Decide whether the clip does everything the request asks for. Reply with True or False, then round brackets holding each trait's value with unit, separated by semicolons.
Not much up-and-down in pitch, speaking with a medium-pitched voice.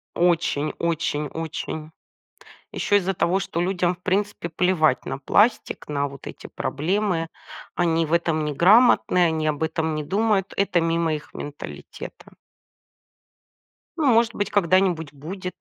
False (3.6 semitones; 170 Hz)